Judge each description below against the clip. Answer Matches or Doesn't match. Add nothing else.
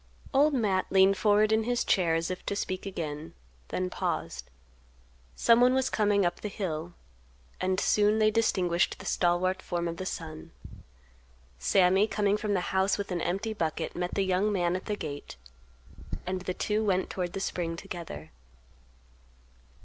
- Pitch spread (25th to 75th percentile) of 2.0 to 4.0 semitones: Matches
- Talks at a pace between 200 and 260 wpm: Doesn't match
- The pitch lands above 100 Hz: Matches